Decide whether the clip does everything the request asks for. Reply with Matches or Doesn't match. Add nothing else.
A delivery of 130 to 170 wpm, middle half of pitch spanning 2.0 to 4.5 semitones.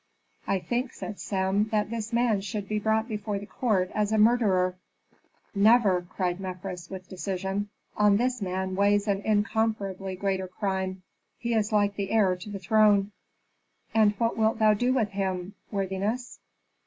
Matches